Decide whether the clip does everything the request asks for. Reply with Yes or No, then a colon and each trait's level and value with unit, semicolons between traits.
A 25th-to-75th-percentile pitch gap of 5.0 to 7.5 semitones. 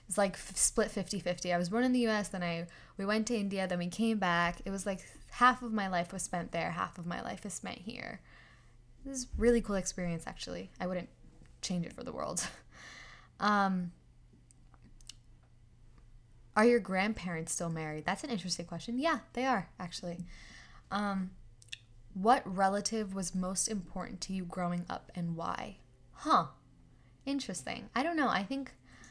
No: average, 4.3 semitones